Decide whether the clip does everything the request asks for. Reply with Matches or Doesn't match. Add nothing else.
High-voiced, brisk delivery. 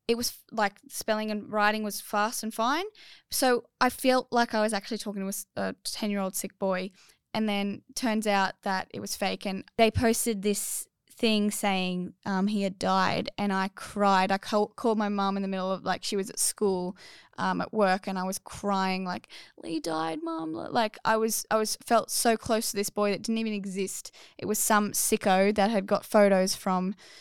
Matches